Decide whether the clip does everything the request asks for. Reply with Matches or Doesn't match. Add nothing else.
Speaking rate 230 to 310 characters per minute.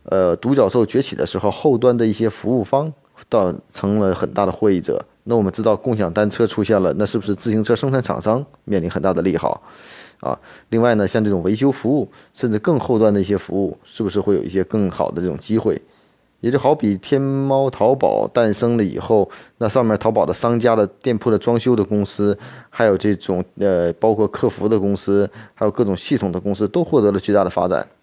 Doesn't match